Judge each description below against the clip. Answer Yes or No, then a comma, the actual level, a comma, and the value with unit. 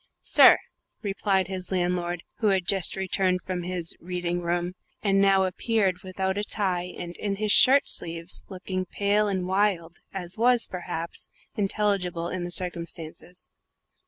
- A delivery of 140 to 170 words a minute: Yes, average, 145 wpm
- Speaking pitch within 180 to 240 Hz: Yes, medium, 185 Hz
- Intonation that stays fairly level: Yes, narrow, 2.0 semitones